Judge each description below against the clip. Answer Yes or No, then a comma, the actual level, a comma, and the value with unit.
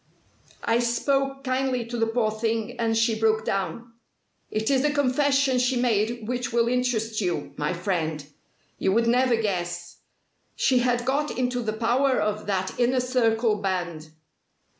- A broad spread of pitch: No, average, 2.9 semitones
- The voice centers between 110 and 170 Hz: No, high, 230 Hz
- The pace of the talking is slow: No, average, 155 wpm